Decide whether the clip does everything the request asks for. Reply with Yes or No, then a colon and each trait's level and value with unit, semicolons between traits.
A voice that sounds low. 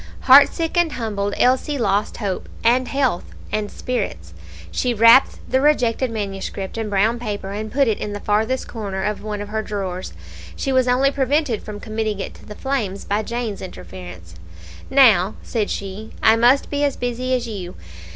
No: high, 220 Hz